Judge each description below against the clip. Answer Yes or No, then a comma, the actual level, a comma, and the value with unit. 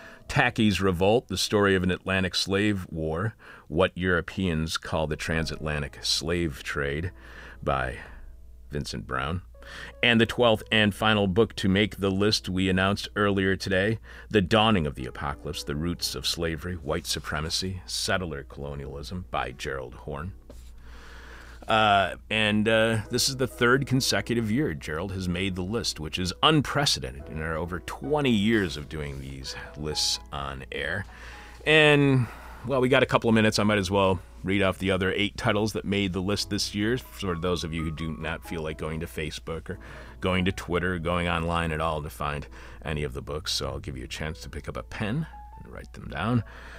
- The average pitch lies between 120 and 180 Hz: No, very low, 90 Hz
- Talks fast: No, average, 185 wpm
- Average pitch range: No, wide, 5.8 semitones